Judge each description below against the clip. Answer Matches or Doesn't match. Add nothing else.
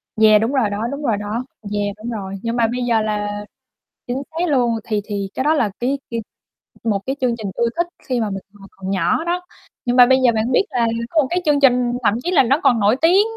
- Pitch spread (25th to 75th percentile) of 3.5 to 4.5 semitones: Matches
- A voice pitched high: Matches